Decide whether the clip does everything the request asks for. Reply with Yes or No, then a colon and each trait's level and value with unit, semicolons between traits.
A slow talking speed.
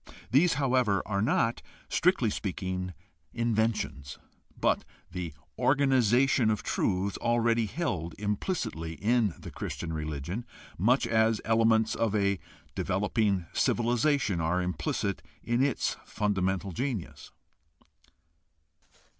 Yes: slow, 100 wpm